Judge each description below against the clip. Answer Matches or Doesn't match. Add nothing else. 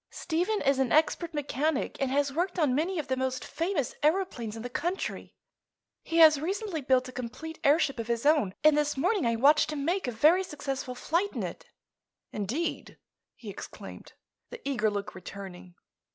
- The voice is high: Matches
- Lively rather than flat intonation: Doesn't match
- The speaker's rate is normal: Matches